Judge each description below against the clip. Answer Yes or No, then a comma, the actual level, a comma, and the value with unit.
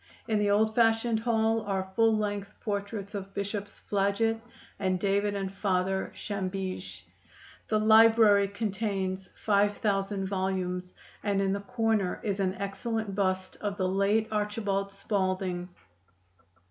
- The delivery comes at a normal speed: No, slow, 130 wpm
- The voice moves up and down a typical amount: No, narrow, 2.0 semitones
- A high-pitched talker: Yes, high, 200 Hz